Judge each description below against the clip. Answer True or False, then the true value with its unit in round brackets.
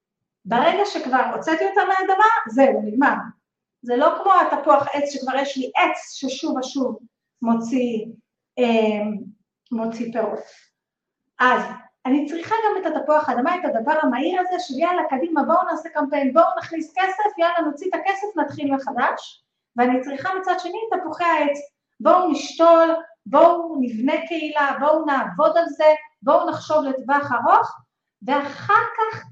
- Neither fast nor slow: True (140 wpm)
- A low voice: False (295 Hz)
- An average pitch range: True (4.8 semitones)